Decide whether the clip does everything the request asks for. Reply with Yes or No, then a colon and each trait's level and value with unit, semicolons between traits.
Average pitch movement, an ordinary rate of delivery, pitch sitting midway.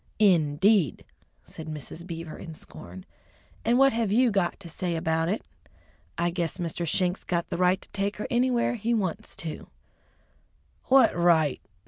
Yes: average, 4.5 semitones; average, 160 wpm; medium, 175 Hz